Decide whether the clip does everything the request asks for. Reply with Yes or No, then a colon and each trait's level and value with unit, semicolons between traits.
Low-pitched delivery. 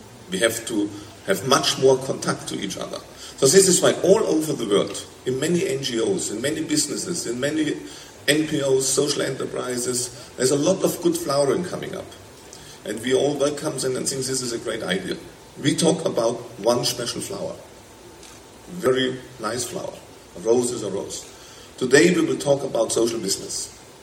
Yes: low, 130 Hz